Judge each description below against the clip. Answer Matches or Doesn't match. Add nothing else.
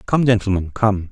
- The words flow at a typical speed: Matches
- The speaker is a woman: Doesn't match